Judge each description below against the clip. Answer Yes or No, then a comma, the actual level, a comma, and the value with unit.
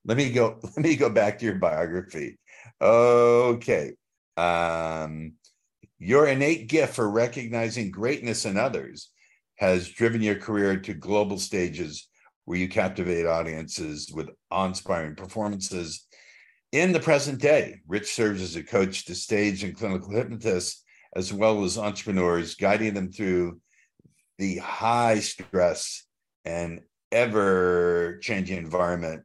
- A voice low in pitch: Yes, very low, 95 Hz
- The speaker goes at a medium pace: No, slow, 125 wpm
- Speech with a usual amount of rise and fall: Yes, average, 4.3 semitones